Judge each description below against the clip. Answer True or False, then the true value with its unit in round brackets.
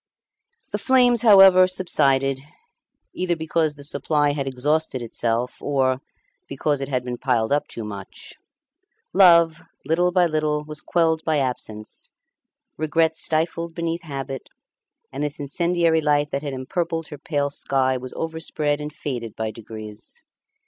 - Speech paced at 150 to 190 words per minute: False (140 wpm)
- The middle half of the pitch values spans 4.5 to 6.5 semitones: False (3.7 semitones)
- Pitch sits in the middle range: True (150 Hz)